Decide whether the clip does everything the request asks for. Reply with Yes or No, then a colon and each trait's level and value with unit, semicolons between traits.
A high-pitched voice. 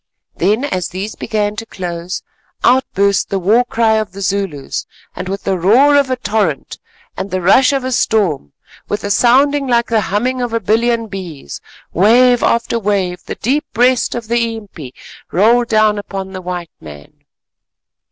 Yes: high, 210 Hz